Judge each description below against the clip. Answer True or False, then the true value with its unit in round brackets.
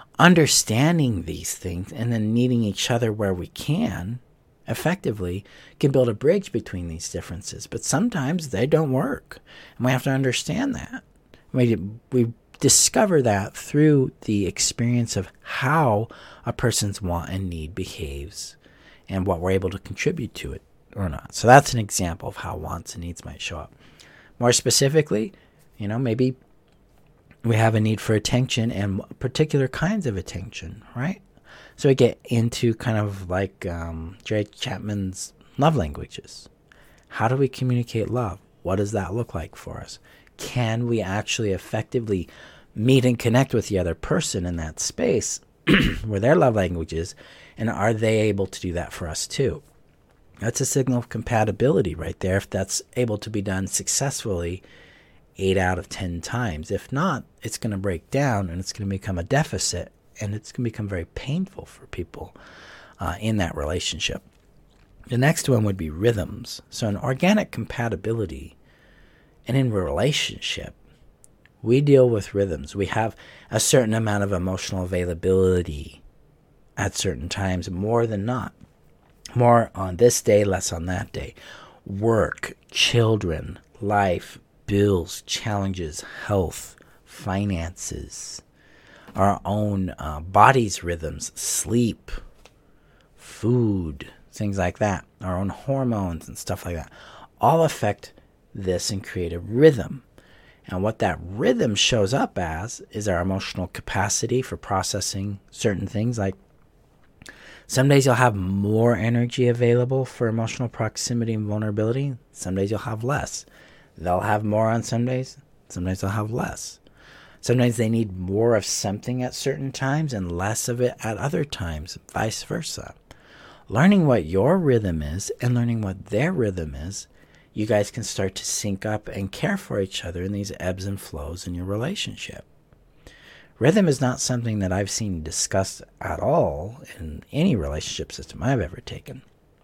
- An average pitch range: True (4.6 semitones)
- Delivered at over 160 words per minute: False (155 wpm)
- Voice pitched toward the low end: True (105 Hz)